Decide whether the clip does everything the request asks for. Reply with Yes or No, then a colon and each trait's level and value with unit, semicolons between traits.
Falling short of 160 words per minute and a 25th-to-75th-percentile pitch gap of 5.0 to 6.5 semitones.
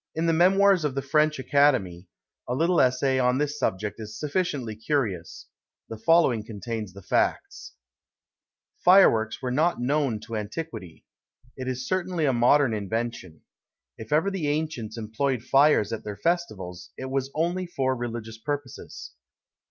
Yes: average, 145 wpm; wide, 5.6 semitones